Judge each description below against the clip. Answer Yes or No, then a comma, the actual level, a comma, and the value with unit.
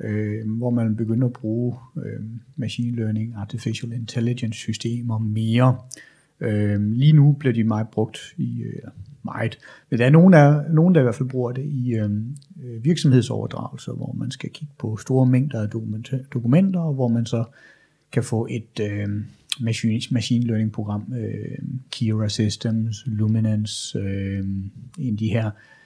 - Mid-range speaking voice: No, low, 115 Hz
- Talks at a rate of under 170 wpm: Yes, average, 155 wpm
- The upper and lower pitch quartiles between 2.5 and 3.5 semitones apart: Yes, average, 2.8 semitones